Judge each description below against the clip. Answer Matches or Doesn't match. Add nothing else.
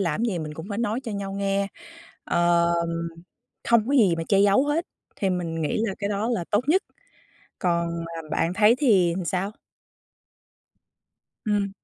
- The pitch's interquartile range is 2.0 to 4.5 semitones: Matches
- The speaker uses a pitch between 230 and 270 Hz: Doesn't match